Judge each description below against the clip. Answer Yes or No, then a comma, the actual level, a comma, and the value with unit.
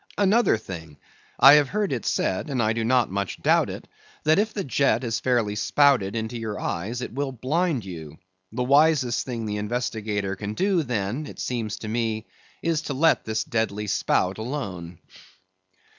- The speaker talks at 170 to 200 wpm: Yes, average, 175 wpm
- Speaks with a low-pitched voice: Yes, low, 115 Hz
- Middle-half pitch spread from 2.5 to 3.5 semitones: No, average, 5.2 semitones